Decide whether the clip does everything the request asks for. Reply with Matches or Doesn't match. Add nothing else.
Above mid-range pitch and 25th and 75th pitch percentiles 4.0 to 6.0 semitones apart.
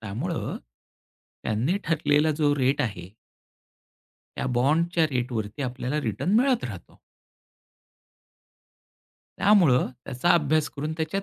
Doesn't match